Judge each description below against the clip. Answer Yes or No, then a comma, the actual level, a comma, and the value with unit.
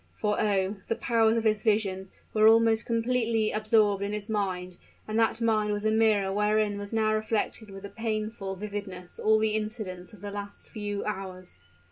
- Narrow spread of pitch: Yes, narrow, 1.6 semitones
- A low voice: No, high, 215 Hz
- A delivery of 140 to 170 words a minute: No, average, 180 wpm